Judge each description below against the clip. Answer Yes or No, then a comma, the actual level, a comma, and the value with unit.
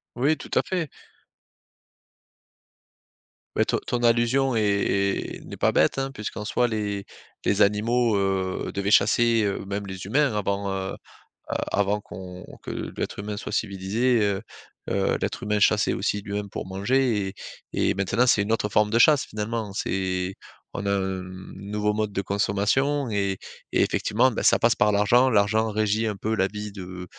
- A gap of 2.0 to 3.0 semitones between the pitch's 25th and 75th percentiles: Yes, narrow, 2.6 semitones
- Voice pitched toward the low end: Yes, low, 105 Hz